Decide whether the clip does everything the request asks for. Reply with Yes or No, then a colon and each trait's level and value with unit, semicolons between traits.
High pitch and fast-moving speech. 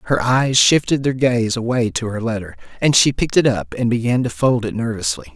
No: low, 120 Hz; fast, 225 wpm